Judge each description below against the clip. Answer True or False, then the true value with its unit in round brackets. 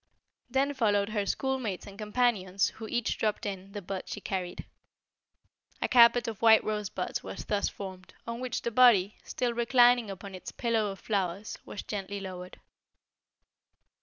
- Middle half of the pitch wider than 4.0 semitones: False (3.3 semitones)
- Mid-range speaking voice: False (210 Hz)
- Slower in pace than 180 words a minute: True (155 wpm)